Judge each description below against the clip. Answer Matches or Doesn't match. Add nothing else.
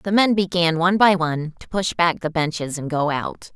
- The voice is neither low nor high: Matches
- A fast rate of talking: Matches